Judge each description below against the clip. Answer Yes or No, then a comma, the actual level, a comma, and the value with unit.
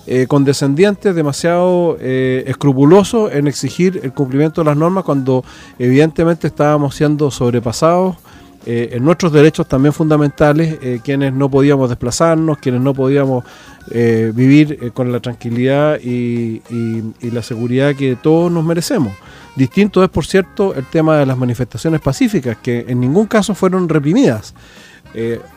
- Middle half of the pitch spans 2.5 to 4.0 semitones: No, average, 4.6 semitones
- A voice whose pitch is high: No, medium, 140 Hz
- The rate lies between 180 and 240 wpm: No, average, 150 wpm